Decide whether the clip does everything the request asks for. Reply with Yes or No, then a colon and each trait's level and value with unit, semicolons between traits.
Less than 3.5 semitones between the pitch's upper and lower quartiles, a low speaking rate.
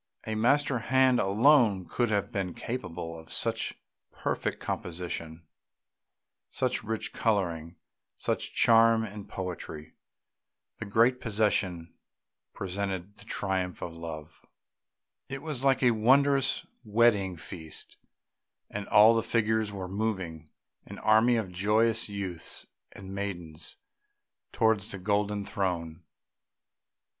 No: average, 4.0 semitones; slow, 115 wpm